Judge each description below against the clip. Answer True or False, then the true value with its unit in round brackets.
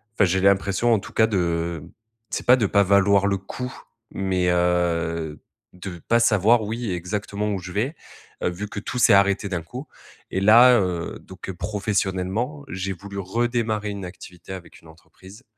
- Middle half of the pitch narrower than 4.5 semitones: True (3.0 semitones)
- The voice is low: True (100 Hz)